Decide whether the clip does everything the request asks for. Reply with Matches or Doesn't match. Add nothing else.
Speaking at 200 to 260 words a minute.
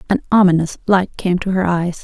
Matches